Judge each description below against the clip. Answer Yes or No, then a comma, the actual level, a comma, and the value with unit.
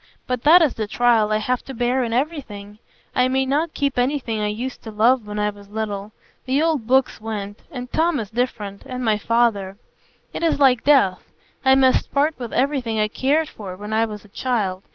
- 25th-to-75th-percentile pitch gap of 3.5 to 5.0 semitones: Yes, average, 4.0 semitones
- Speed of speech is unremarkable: No, fast, 210 wpm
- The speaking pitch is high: Yes, high, 240 Hz